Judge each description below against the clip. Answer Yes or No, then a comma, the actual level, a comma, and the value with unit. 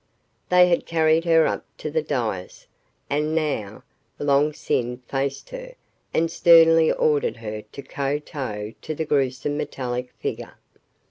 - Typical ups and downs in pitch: Yes, average, 3.7 semitones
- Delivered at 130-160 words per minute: Yes, slow, 135 wpm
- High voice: No, medium, 145 Hz